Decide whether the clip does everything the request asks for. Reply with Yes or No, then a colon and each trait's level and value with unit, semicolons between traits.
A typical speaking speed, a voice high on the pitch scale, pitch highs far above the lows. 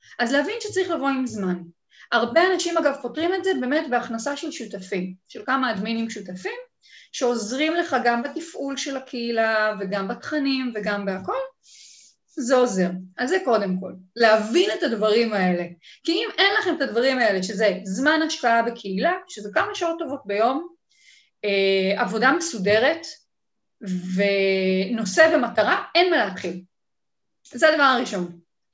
Yes: average, 140 wpm; high, 240 Hz; wide, 7.7 semitones